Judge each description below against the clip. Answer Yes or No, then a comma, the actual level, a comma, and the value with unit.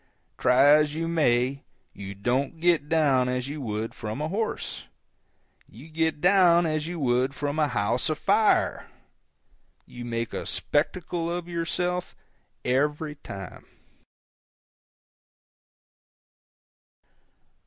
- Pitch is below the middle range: No, medium, 150 Hz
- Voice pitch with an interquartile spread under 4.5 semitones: No, average, 4.9 semitones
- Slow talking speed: Yes, slow, 110 wpm